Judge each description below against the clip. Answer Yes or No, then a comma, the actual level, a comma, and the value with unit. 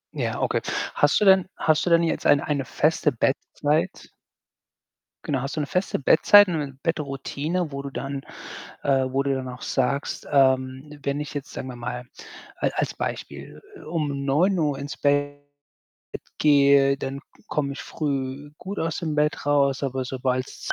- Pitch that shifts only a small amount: Yes, narrow, 2.0 semitones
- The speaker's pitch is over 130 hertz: Yes, medium, 140 Hz